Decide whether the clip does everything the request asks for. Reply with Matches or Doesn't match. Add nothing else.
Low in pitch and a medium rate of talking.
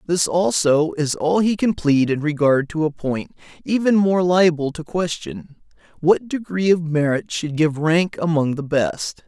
Doesn't match